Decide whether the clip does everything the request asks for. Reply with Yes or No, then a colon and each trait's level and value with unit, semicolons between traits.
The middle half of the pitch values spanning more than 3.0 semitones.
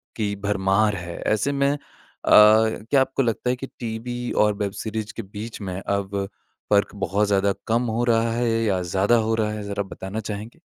No: narrow, 2.5 semitones